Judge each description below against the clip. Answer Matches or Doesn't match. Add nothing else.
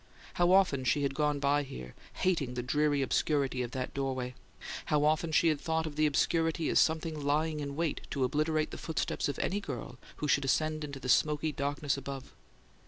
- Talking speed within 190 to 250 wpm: Matches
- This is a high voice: Doesn't match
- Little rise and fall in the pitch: Matches